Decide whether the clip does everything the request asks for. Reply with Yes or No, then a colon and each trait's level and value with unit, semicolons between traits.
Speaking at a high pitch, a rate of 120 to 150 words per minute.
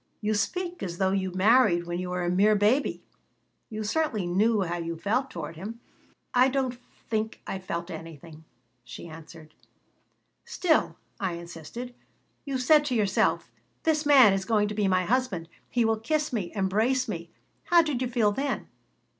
No: high, 210 Hz; average, 170 wpm